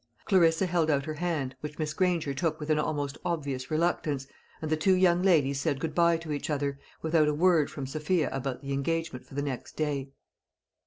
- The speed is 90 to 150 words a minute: No, fast, 205 wpm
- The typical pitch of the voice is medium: Yes, medium, 155 Hz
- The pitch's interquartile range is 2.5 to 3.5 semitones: Yes, average, 3.0 semitones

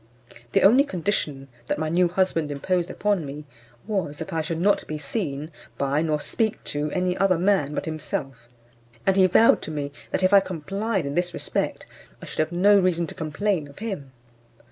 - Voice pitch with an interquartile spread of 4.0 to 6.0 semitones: Yes, average, 4.5 semitones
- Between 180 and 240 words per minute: Yes, average, 190 wpm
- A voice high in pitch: No, medium, 170 Hz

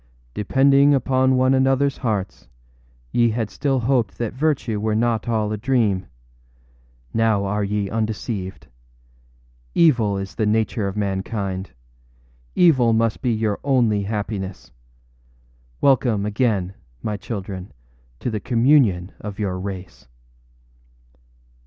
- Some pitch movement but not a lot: Yes, average, 4.0 semitones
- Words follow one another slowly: Yes, slow, 115 wpm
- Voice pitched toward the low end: Yes, low, 110 Hz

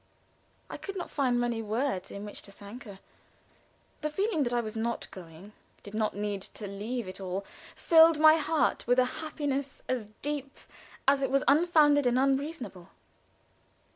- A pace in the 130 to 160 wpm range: No, average, 170 wpm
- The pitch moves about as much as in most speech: No, wide, 5.9 semitones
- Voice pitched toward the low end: No, very high, 250 Hz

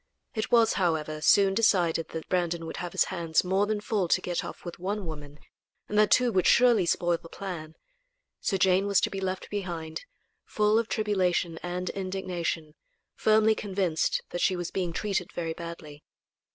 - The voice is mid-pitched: Yes, medium, 180 Hz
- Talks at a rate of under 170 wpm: No, average, 180 wpm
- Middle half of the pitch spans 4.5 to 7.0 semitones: No, average, 3.2 semitones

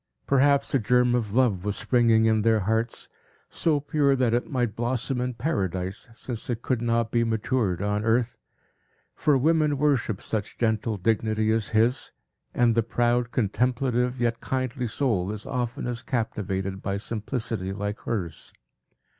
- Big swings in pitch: No, average, 2.7 semitones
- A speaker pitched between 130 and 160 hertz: No, low, 115 Hz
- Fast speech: No, average, 150 wpm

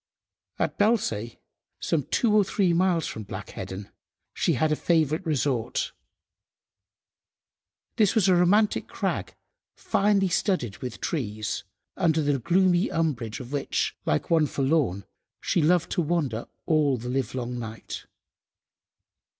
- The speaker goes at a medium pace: No, slow, 125 wpm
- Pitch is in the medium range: Yes, medium, 150 Hz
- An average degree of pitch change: No, wide, 6.8 semitones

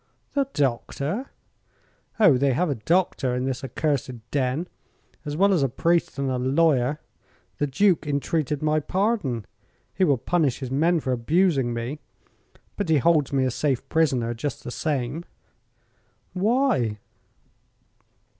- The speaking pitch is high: No, medium, 145 Hz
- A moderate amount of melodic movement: Yes, average, 4.8 semitones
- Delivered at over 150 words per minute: No, average, 140 wpm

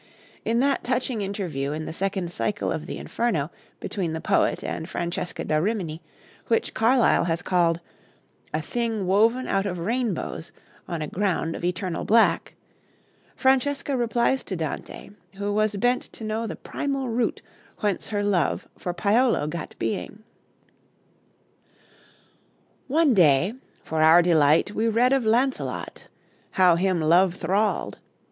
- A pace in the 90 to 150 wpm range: Yes, average, 140 wpm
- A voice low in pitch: No, high, 200 Hz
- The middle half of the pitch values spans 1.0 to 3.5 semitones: No, average, 5.2 semitones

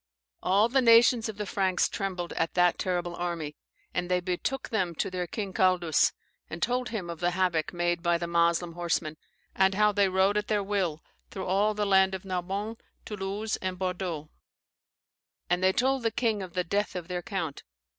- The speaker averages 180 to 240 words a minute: Yes, average, 190 wpm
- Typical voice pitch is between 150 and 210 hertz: Yes, medium, 185 Hz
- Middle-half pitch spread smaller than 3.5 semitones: Yes, average, 2.9 semitones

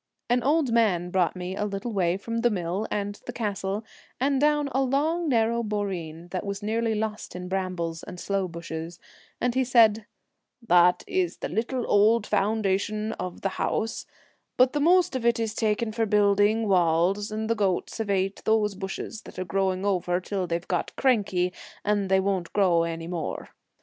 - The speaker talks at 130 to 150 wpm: No, average, 185 wpm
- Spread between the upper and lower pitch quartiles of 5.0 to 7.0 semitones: No, average, 3.7 semitones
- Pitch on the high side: Yes, high, 205 Hz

